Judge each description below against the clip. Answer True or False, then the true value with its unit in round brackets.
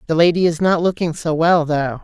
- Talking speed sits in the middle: False (235 wpm)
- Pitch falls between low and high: True (165 Hz)